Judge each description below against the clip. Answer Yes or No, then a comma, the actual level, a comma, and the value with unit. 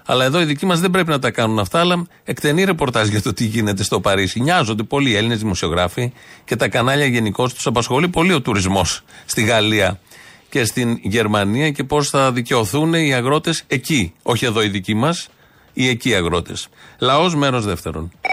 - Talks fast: Yes, fast, 185 wpm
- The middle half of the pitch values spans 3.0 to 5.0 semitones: No, wide, 5.4 semitones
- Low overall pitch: Yes, low, 125 Hz